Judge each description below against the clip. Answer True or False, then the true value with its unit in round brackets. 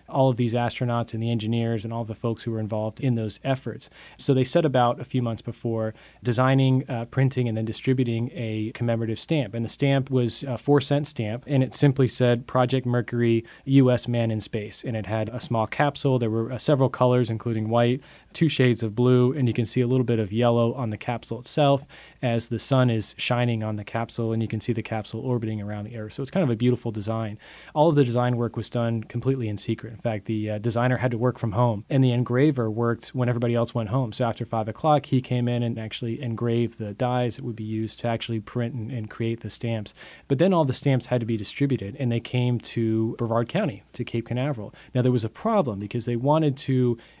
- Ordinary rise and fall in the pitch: False (2.1 semitones)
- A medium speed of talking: False (240 wpm)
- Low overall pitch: True (120 Hz)